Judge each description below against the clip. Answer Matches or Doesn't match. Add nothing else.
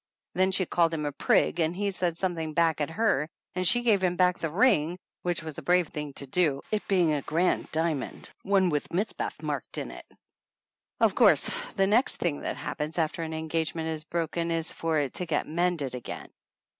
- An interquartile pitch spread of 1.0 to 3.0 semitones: Matches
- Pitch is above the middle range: Doesn't match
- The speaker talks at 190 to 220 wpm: Matches